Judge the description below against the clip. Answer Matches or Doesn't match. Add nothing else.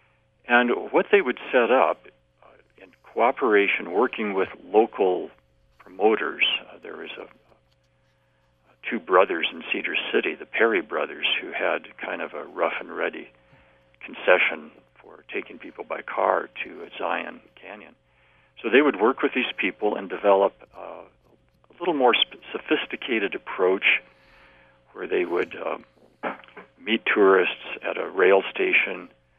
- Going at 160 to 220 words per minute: Doesn't match